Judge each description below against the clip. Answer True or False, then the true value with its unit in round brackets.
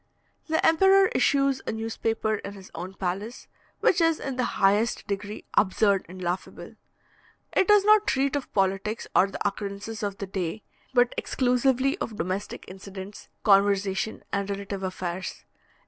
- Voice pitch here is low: False (205 Hz)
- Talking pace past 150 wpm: False (145 wpm)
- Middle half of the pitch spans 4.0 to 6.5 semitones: True (4.7 semitones)